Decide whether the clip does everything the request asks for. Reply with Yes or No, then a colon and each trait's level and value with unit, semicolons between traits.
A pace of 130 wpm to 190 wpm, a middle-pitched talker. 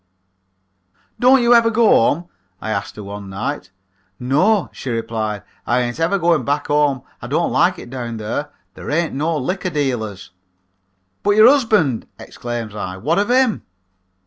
Yes: average, 160 wpm; medium, 145 Hz